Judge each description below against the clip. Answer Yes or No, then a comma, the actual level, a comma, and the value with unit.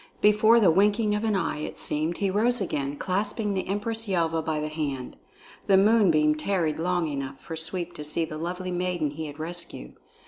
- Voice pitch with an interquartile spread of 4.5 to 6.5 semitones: Yes, average, 4.8 semitones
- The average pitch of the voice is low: No, medium, 175 Hz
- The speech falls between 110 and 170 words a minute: No, average, 195 wpm